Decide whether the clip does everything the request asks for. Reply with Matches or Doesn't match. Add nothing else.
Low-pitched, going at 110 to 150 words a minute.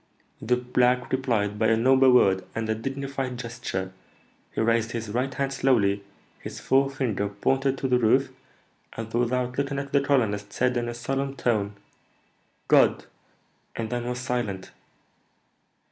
Matches